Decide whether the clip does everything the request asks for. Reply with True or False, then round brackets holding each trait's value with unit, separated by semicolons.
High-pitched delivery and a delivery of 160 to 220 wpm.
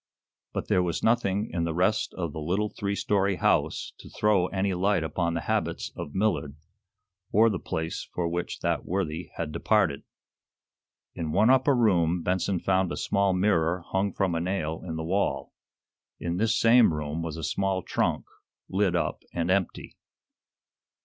False (90 Hz; 170 wpm)